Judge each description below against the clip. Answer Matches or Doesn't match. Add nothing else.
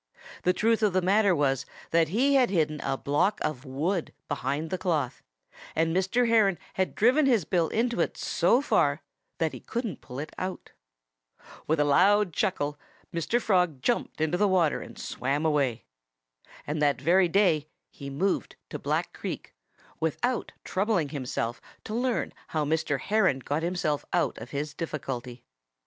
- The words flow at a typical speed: Matches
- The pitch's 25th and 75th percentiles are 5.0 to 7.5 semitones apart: Matches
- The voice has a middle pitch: Matches